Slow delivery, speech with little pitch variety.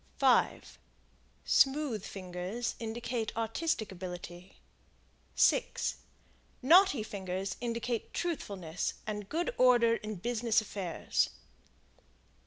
No: slow, 80 wpm; average, 4.2 semitones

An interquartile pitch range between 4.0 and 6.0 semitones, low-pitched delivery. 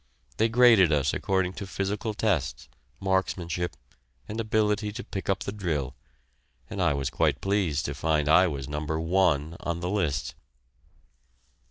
Yes: average, 5.1 semitones; very low, 90 Hz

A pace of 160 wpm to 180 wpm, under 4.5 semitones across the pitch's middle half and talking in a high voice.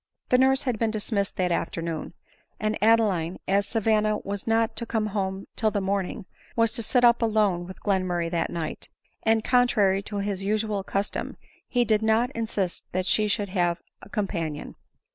Yes: average, 175 wpm; average, 2.8 semitones; high, 205 Hz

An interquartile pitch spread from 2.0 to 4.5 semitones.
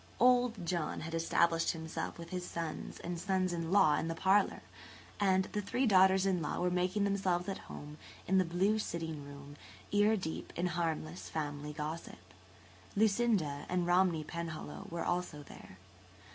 Yes: average, 3.0 semitones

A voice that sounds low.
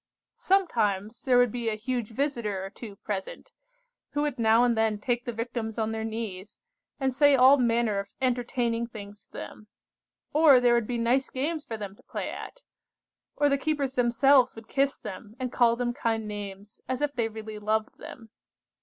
No: high, 235 Hz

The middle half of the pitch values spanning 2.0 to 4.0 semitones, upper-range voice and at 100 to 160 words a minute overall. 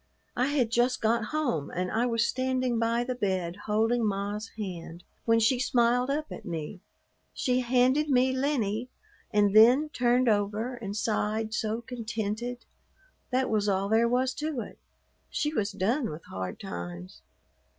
Yes: average, 3.5 semitones; high, 230 Hz; average, 155 wpm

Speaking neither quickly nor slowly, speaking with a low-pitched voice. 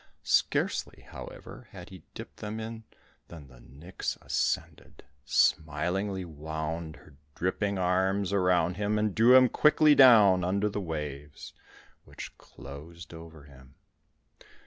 No: slow, 125 wpm; very low, 90 Hz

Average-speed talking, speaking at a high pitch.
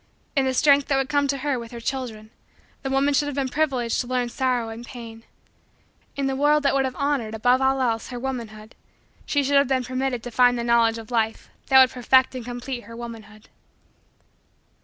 No: fast, 210 wpm; very high, 255 Hz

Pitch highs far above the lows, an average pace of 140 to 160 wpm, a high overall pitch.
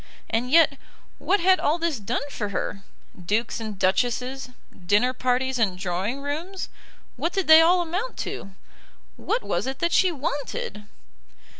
Yes: wide, 7.2 semitones; average, 150 wpm; very high, 265 Hz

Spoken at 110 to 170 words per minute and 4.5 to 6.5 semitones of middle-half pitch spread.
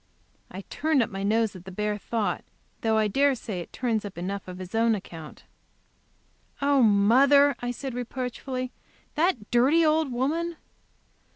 Yes: average, 160 wpm; wide, 5.4 semitones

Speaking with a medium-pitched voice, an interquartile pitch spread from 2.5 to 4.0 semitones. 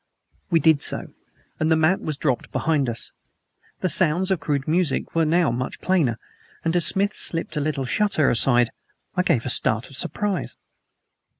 No: medium, 155 Hz; average, 4.7 semitones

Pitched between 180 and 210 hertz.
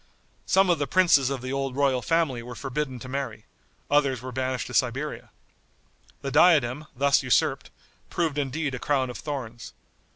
No: low, 135 Hz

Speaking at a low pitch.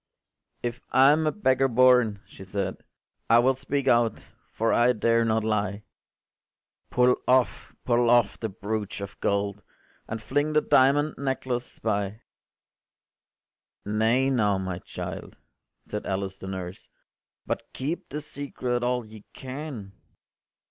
Yes: low, 120 Hz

